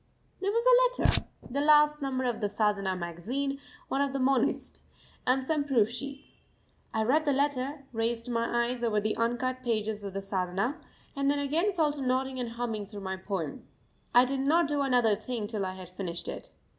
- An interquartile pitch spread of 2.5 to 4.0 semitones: No, average, 4.9 semitones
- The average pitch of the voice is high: Yes, very high, 250 Hz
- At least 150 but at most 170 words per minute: No, average, 195 wpm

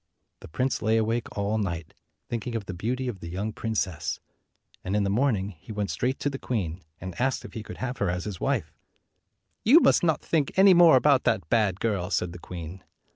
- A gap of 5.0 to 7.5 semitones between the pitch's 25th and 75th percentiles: Yes, wide, 5.4 semitones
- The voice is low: Yes, low, 110 Hz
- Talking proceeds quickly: Yes, fast, 220 wpm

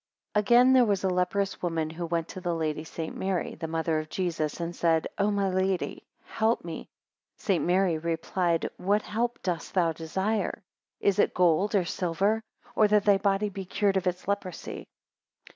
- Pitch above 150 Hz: Yes, medium, 185 Hz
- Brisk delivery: No, average, 180 wpm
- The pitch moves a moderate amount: Yes, average, 3.2 semitones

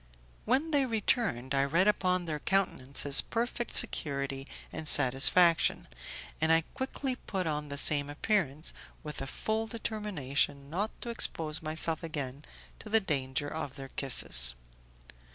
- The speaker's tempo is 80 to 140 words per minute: Yes, slow, 135 wpm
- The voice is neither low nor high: Yes, medium, 155 Hz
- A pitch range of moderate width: No, wide, 7.1 semitones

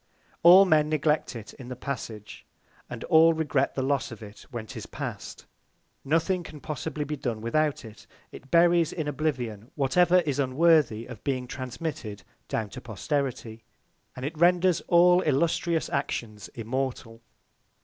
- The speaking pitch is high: No, medium, 140 Hz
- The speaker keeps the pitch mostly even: No, average, 5.3 semitones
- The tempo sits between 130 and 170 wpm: Yes, average, 150 wpm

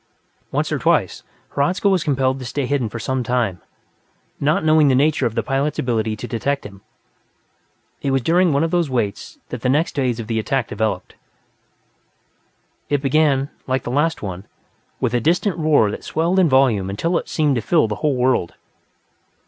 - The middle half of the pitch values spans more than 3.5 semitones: Yes, average, 4.9 semitones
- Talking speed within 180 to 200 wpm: Yes, average, 185 wpm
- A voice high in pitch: No, low, 135 Hz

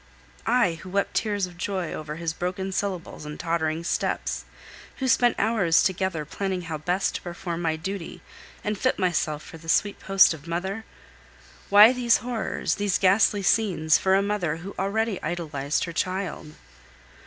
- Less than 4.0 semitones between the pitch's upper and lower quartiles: Yes, average, 3.5 semitones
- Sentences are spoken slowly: No, average, 165 wpm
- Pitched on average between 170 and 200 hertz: Yes, medium, 185 Hz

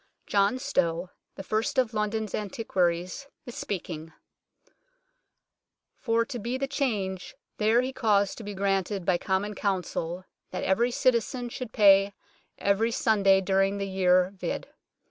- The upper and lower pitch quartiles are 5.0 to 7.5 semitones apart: No, average, 3.5 semitones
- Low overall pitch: No, high, 200 Hz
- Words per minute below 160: Yes, average, 140 wpm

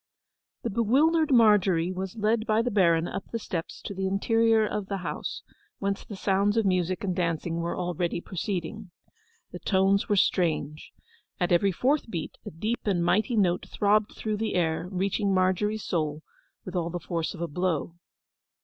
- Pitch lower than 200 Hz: Yes, high, 190 Hz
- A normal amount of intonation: Yes, average, 3.6 semitones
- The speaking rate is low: No, average, 175 wpm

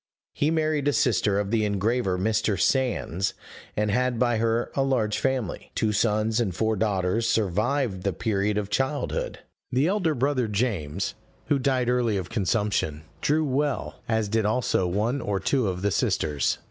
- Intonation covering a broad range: No, average, 4.2 semitones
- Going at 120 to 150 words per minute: No, average, 165 wpm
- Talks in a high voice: No, low, 110 Hz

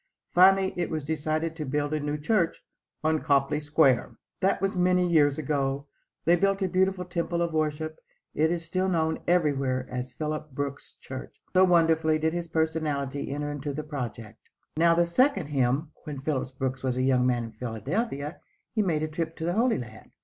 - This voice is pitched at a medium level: Yes, medium, 155 Hz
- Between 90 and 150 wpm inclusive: No, average, 185 wpm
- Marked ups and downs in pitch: No, average, 3.5 semitones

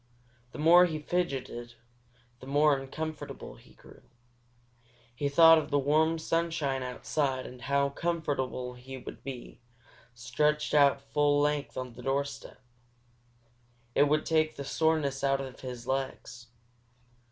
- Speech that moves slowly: Yes, slow, 130 wpm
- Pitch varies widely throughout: No, average, 2.7 semitones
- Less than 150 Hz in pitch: Yes, medium, 140 Hz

